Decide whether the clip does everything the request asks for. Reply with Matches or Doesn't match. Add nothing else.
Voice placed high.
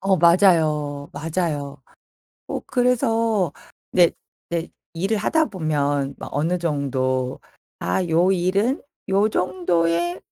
Doesn't match